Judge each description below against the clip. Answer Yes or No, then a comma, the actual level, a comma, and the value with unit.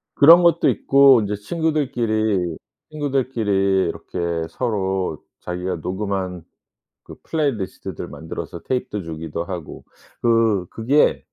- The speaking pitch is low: Yes, low, 105 Hz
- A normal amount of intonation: No, wide, 6.4 semitones